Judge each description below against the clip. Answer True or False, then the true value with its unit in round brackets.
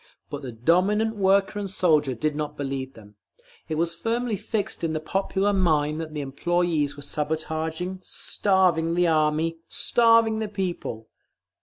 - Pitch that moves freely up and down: False (4.4 semitones)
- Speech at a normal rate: True (150 wpm)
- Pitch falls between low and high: True (165 Hz)